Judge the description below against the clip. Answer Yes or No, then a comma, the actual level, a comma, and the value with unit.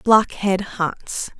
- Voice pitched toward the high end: Yes, high, 200 Hz